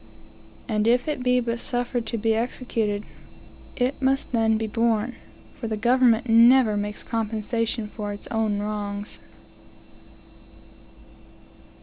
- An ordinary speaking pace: No, slow, 120 wpm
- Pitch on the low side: No, high, 225 Hz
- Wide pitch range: No, narrow, 2.4 semitones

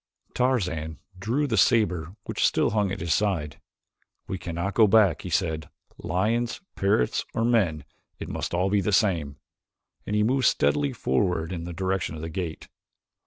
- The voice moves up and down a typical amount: Yes, average, 4.6 semitones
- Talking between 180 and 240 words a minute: No, average, 165 wpm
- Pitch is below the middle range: Yes, very low, 95 Hz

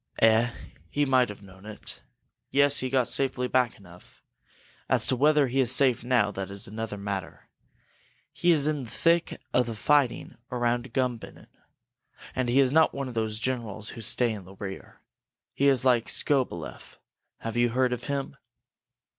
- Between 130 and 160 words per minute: No, average, 170 wpm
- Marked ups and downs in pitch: No, average, 3.7 semitones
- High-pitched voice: No, low, 125 Hz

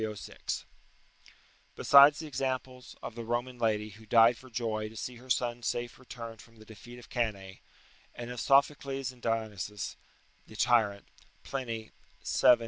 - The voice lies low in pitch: Yes, low, 120 Hz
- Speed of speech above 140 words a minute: Yes, average, 155 wpm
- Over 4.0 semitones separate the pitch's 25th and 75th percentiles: No, narrow, 2.5 semitones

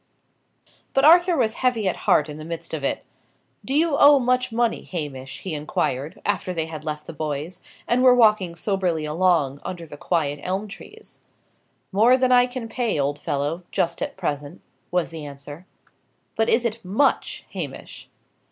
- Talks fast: No, average, 170 wpm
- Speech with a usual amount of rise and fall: No, wide, 7.9 semitones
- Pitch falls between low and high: Yes, medium, 180 Hz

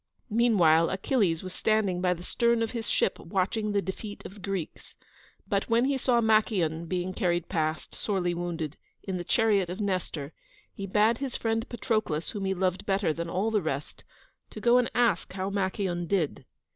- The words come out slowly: No, average, 185 wpm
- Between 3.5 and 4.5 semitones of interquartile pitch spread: Yes, average, 4.0 semitones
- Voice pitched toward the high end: Yes, high, 195 Hz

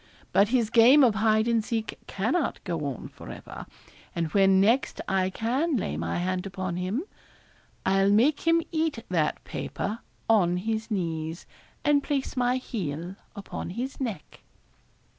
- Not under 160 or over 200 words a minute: No, average, 150 wpm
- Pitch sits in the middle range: No, high, 215 Hz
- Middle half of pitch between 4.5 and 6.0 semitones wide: Yes, average, 5.2 semitones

